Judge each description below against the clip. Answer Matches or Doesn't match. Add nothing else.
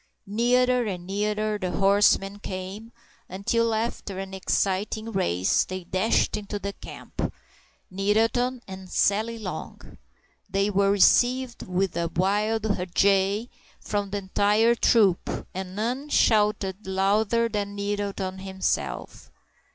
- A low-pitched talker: Doesn't match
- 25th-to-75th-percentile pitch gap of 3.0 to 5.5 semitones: Doesn't match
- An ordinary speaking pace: Doesn't match